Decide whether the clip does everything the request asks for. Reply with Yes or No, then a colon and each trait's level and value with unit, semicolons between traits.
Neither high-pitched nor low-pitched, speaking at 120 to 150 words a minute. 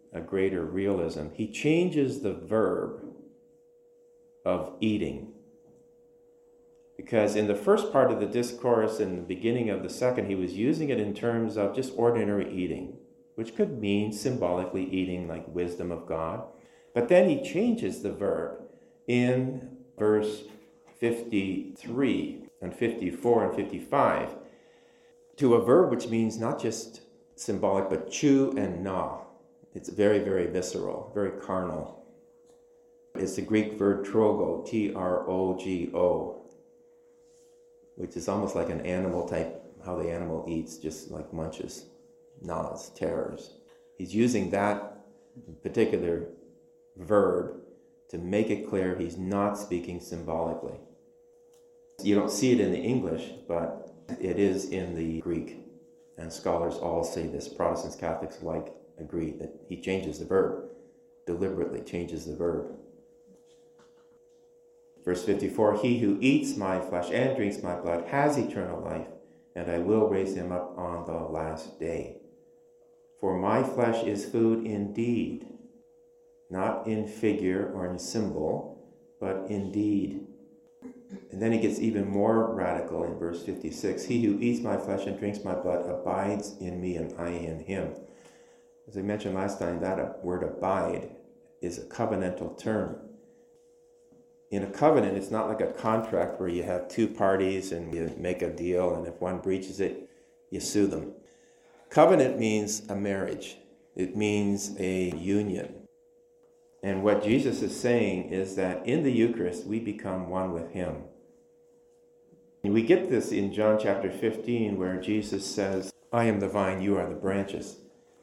No: low, 105 Hz; average, 145 wpm